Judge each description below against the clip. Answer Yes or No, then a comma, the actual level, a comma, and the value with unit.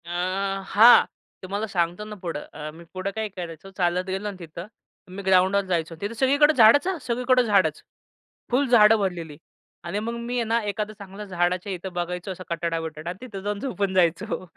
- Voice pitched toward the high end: Yes, high, 195 Hz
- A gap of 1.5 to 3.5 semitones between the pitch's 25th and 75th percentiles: No, average, 3.9 semitones